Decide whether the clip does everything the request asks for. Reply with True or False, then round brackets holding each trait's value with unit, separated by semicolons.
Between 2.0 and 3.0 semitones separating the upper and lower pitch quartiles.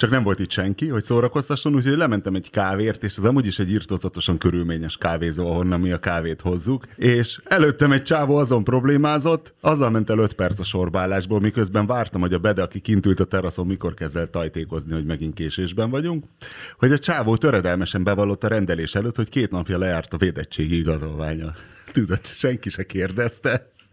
False (5.4 semitones)